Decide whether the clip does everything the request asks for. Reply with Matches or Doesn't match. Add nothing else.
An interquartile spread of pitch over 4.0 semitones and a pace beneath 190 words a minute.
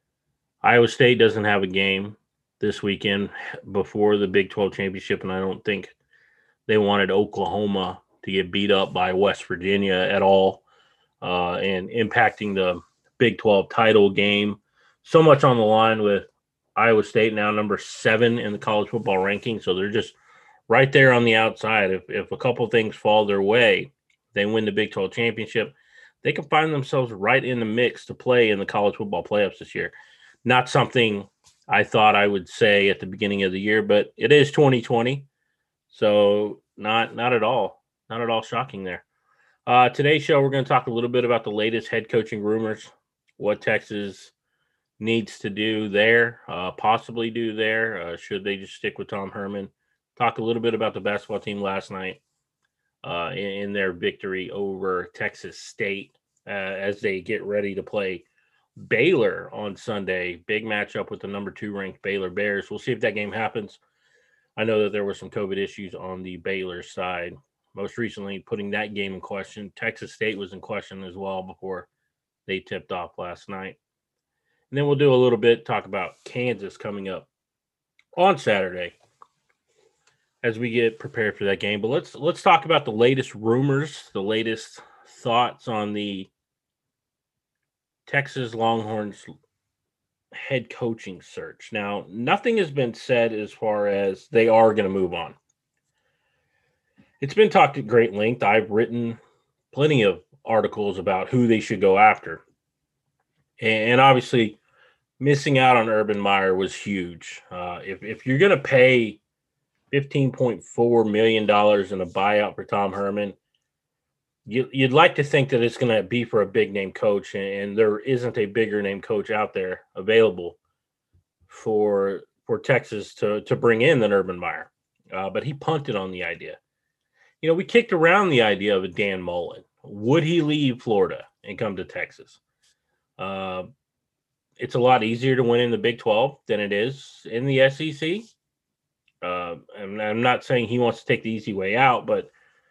Doesn't match